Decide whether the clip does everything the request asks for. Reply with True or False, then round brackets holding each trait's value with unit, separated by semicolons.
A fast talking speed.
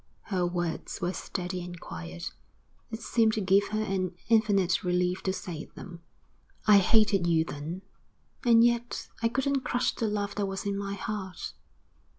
False (165 wpm)